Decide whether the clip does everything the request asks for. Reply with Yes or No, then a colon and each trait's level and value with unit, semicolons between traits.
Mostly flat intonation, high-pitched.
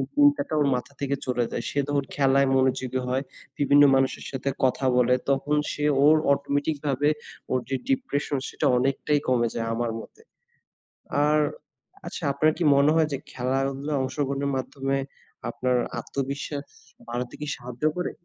No: narrow, 1.9 semitones; medium, 140 Hz